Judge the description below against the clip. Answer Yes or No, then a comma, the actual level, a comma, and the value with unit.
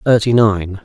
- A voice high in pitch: No, low, 105 Hz